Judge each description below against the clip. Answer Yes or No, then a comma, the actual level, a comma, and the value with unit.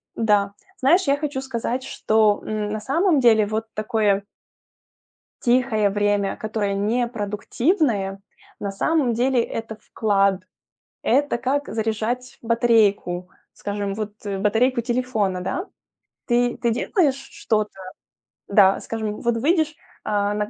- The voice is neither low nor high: No, high, 220 Hz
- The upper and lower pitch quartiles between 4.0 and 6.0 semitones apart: No, average, 3.5 semitones